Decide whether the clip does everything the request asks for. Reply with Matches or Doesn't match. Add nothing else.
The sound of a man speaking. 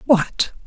Doesn't match